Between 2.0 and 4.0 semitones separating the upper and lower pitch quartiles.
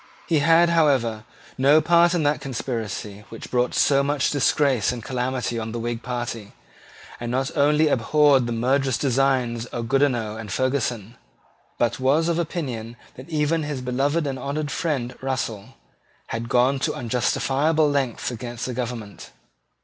Yes: average, 3.5 semitones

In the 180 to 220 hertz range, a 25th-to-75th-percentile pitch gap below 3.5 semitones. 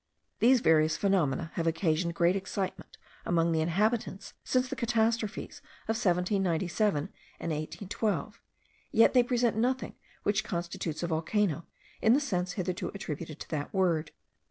No: medium, 185 Hz; average, 5.0 semitones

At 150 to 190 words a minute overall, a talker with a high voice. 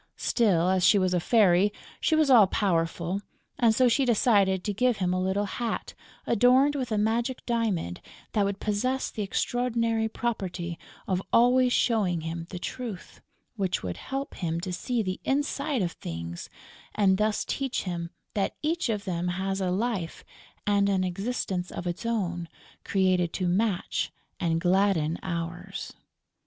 Yes: average, 160 wpm; high, 200 Hz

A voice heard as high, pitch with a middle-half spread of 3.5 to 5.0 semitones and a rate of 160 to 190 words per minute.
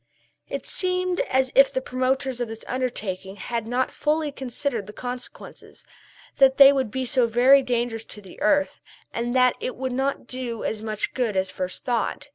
No: very high, 250 Hz; average, 2.7 semitones; average, 180 wpm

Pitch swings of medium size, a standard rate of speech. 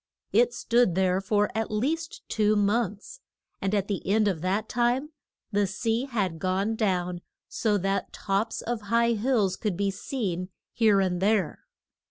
Yes: average, 3.2 semitones; average, 160 wpm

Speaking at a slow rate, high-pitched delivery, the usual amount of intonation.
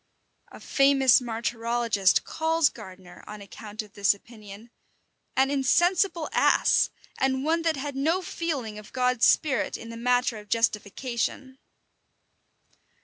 Yes: slow, 125 wpm; high, 245 Hz; average, 4.5 semitones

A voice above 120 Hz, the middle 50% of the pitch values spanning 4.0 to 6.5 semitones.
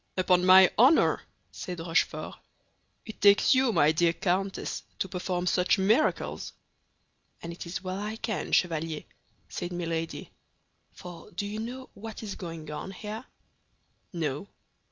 No: medium, 185 Hz; average, 3.6 semitones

